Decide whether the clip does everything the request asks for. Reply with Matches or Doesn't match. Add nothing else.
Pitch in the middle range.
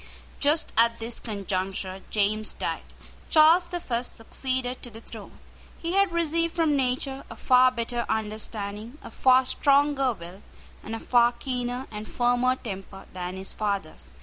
Doesn't match